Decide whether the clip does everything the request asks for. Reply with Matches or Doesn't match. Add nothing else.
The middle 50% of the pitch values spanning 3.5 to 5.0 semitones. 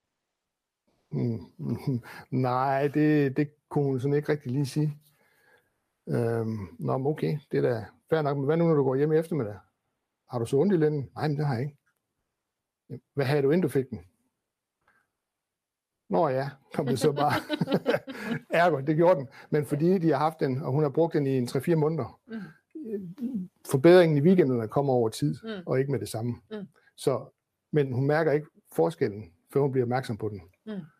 Matches